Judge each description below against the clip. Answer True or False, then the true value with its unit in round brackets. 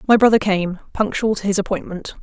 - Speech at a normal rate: True (190 wpm)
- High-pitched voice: True (200 Hz)